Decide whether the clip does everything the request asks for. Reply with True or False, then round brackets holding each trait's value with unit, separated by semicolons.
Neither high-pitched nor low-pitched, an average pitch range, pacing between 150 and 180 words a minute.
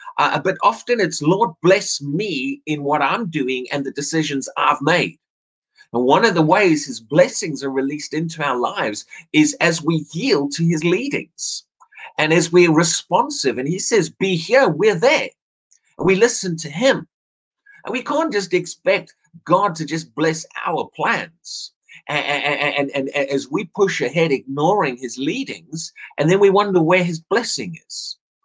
True (165 Hz; 4.7 semitones; 175 wpm)